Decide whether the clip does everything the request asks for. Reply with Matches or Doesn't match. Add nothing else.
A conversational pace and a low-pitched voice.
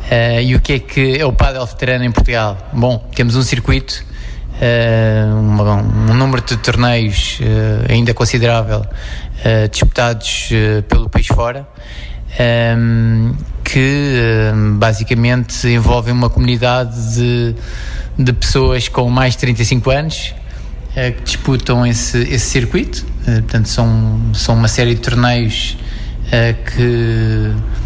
Matches